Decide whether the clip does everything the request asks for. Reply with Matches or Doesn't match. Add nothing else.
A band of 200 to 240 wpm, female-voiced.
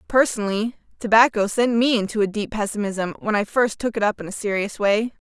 Matches